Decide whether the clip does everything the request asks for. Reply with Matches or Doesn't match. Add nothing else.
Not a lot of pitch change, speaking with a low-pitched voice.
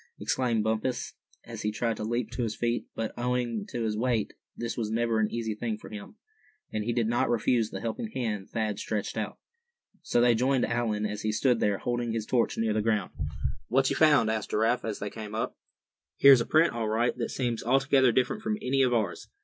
Matches